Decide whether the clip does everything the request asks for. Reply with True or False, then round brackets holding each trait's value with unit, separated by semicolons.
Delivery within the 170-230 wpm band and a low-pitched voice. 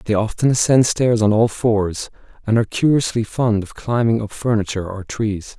True (185 wpm; 110 Hz)